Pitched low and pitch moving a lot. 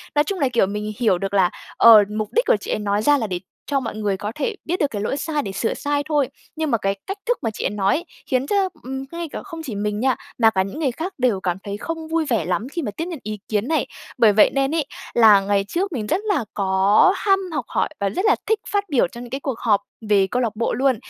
No: high, 245 Hz; wide, 7.2 semitones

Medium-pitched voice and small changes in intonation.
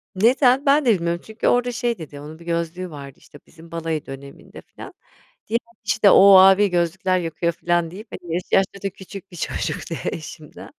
No: medium, 175 Hz; average, 3.5 semitones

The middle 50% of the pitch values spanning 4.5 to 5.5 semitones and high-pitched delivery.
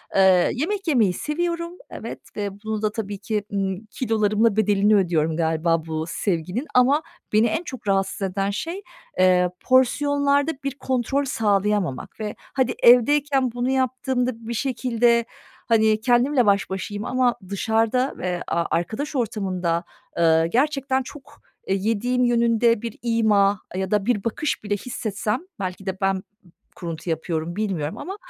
Yes: average, 4.8 semitones; high, 220 Hz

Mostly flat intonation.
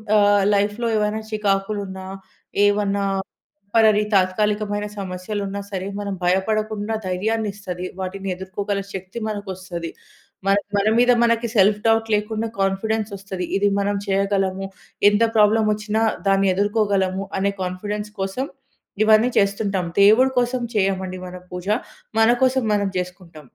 Yes: narrow, 2.0 semitones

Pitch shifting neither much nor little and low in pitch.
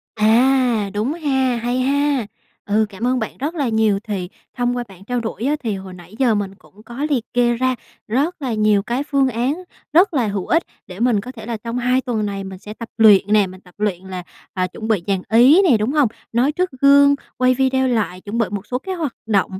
No: average, 4.2 semitones; high, 235 Hz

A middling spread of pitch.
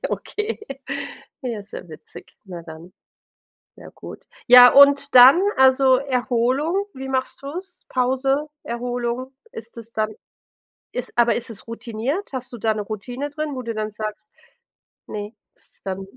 Yes: average, 3.7 semitones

